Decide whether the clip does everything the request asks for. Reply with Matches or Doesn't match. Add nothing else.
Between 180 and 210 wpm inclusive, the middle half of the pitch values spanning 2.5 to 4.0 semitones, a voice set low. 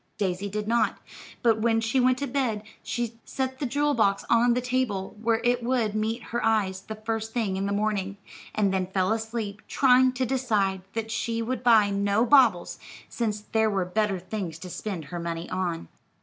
Doesn't match